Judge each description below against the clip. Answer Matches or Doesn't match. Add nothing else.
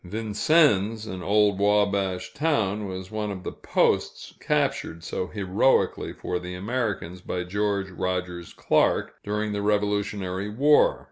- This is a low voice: Matches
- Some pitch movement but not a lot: Doesn't match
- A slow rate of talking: Matches